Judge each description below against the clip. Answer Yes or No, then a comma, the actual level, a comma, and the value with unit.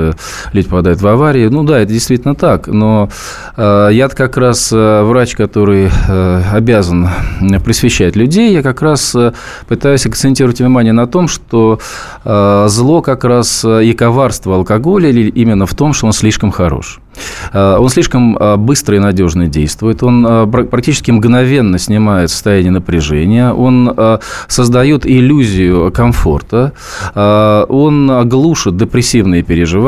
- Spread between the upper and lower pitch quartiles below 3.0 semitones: No, average, 3.8 semitones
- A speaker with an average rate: Yes, average, 120 wpm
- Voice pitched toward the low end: Yes, low, 115 Hz